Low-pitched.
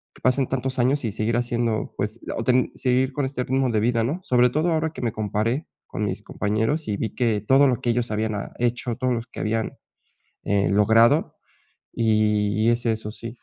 Yes: low, 115 Hz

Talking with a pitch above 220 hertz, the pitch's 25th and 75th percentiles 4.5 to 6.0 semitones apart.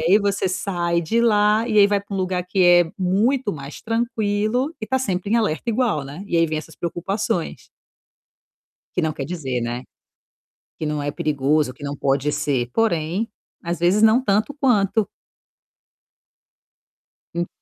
No: medium, 185 Hz; wide, 5.6 semitones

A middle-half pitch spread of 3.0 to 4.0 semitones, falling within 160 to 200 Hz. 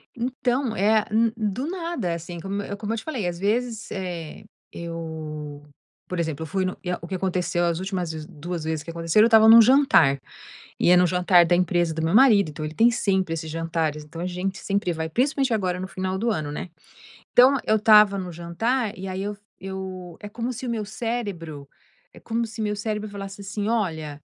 No: average, 4.7 semitones; high, 190 Hz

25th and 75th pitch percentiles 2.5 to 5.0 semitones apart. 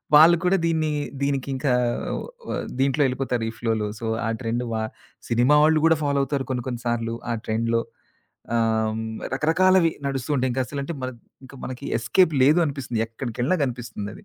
Yes: average, 4.1 semitones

